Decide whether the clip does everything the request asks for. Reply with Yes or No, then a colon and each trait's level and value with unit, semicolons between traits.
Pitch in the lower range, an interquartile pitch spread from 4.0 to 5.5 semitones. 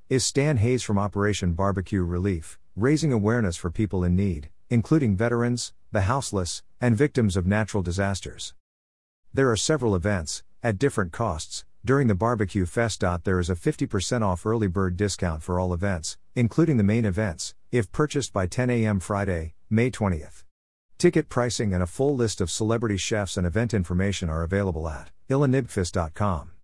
Yes: low, 100 Hz; average, 4.7 semitones